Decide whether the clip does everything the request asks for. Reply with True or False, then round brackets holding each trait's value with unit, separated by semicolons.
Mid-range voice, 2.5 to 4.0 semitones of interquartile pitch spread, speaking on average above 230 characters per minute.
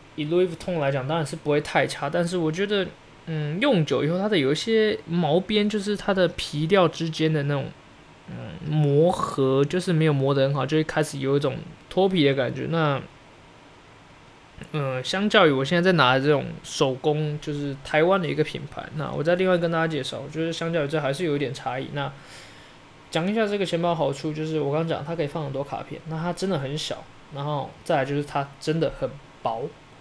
True (155 Hz; 3.3 semitones; 315 characters per minute)